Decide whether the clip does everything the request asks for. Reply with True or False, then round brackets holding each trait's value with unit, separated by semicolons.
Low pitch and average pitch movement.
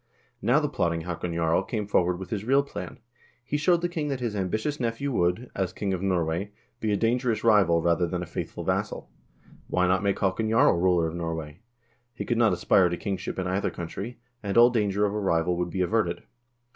True (95 Hz; 4.6 semitones)